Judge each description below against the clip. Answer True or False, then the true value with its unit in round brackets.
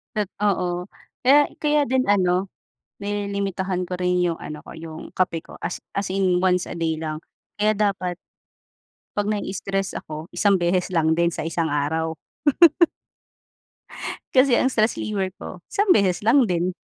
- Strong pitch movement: False (3.0 semitones)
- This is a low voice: False (185 Hz)